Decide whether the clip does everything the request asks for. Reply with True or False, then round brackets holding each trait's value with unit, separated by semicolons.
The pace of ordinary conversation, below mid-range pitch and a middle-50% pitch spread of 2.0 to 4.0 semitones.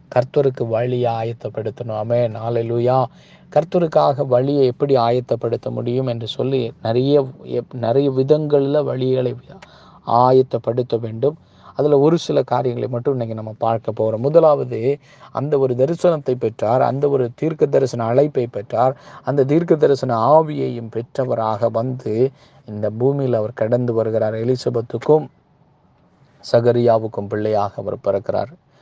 True (110 wpm; 125 Hz; 3.4 semitones)